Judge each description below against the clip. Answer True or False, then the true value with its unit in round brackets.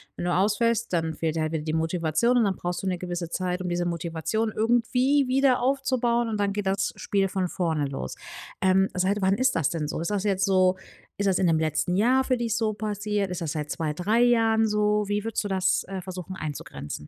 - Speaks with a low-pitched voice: False (190 Hz)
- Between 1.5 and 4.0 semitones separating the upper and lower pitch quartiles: False (4.5 semitones)